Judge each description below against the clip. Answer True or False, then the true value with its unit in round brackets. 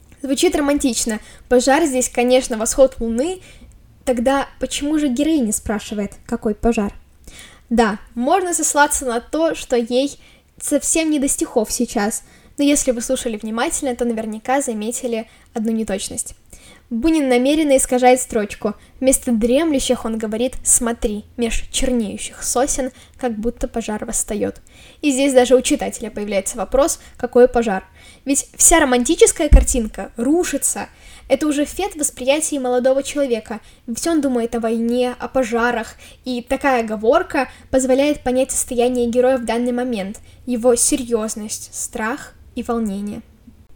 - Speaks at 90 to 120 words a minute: False (130 wpm)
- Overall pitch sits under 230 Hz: False (250 Hz)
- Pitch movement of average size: True (3.0 semitones)